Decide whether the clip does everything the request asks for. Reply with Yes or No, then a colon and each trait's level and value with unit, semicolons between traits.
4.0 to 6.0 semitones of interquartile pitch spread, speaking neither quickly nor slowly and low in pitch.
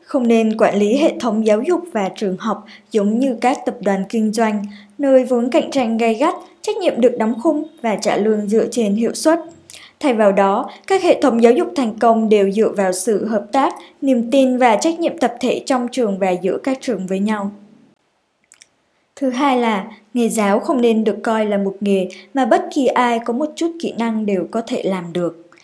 No: average, 4.3 semitones; average, 220 wpm; high, 230 Hz